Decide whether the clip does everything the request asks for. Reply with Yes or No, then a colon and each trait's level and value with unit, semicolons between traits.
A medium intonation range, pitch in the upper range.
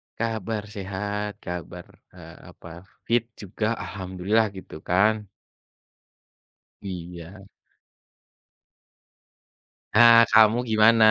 No: average, 3.0 semitones; low, 105 Hz